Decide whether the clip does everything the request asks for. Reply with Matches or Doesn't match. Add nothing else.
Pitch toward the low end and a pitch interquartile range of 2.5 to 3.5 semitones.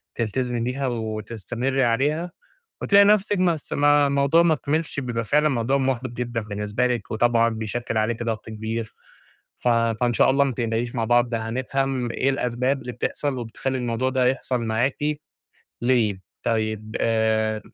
Matches